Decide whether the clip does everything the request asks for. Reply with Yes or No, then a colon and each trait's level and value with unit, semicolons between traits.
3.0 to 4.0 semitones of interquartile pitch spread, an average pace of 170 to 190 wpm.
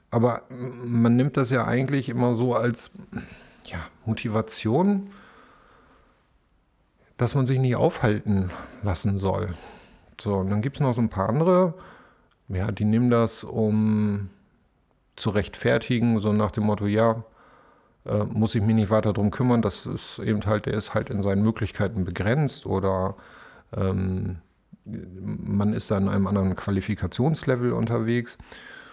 No: average, 3.3 semitones; average, 145 wpm